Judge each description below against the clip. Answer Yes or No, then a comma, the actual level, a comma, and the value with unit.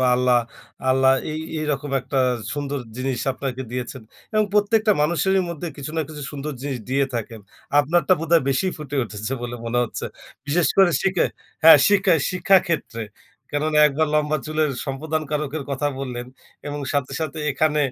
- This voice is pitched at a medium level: Yes, medium, 145 Hz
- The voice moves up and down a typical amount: Yes, average, 3.1 semitones